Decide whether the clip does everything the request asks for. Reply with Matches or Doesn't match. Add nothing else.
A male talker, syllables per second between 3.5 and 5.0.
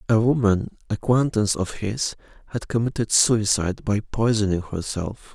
Matches